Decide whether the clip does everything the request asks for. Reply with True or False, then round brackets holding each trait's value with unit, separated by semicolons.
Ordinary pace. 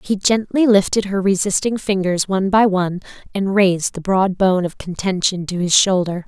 True (180 wpm)